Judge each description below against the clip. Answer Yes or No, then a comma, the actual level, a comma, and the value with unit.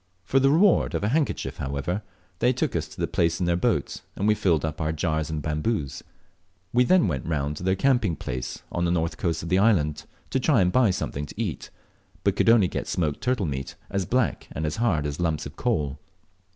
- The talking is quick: Yes, fast, 225 wpm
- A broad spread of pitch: Yes, wide, 6.1 semitones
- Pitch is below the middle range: Yes, very low, 85 Hz